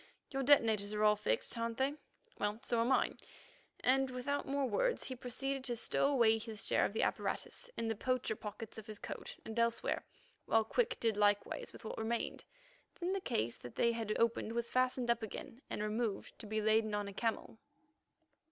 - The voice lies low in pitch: No, high, 230 Hz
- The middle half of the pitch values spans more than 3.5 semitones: No, average, 2.9 semitones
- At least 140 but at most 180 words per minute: No, average, 195 wpm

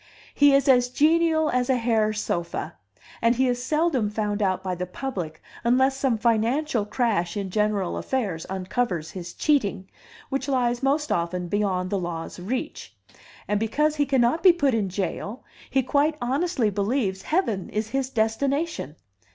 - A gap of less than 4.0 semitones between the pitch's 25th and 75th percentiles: No, wide, 5.6 semitones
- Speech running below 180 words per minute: Yes, average, 160 wpm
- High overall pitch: Yes, high, 235 Hz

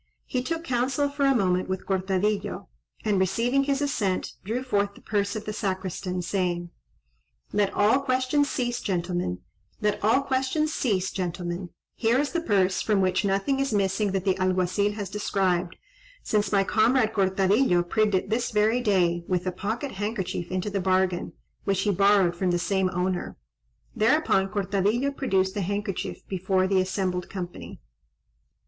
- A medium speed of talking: Yes, average, 150 wpm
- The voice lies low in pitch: No, high, 200 Hz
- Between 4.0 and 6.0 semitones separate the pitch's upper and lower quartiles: No, average, 3.2 semitones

